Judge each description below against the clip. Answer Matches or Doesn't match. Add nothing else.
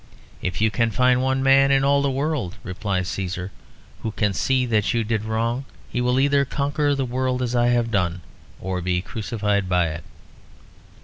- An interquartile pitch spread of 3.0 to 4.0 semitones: Doesn't match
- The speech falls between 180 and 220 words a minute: Matches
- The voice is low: Matches